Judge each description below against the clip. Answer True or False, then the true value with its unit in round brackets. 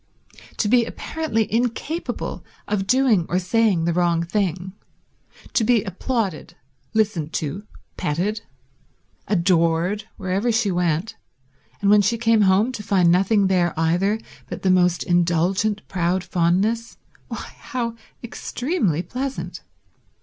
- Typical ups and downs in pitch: True (4.3 semitones)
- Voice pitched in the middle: False (195 Hz)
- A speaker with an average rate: False (120 wpm)